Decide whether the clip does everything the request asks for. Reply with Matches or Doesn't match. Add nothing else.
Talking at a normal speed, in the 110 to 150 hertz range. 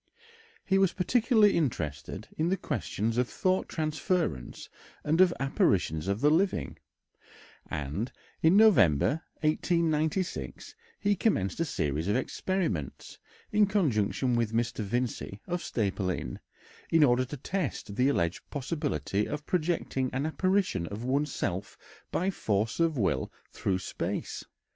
Doesn't match